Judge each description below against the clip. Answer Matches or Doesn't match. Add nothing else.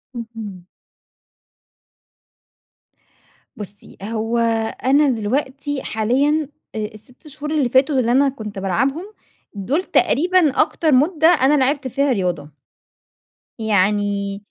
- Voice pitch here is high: Matches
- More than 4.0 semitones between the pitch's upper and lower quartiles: Matches